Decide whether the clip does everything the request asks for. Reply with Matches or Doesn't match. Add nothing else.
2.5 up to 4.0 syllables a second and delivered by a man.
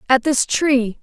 Doesn't match